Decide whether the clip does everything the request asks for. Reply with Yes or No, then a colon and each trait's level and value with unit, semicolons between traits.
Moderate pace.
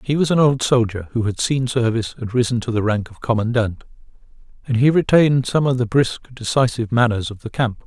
No: fast, 215 wpm